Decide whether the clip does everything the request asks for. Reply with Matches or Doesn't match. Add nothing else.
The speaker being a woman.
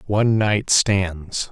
Doesn't match